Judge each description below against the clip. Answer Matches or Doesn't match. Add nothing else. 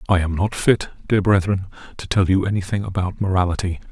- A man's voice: Matches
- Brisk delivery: Doesn't match